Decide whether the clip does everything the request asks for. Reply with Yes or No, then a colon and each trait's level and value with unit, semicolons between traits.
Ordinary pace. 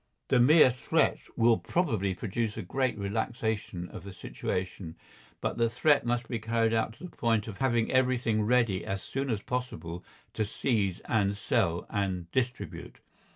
Yes: average, 160 wpm